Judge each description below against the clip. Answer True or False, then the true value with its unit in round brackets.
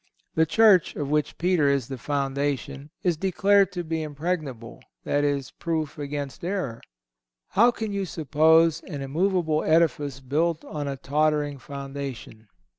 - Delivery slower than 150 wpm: True (135 wpm)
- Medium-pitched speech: True (150 Hz)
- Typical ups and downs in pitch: True (3.3 semitones)